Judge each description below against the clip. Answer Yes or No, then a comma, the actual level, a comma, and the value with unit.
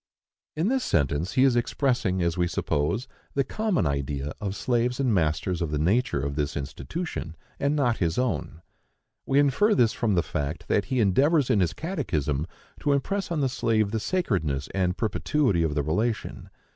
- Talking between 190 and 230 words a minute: No, average, 180 wpm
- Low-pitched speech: Yes, low, 105 Hz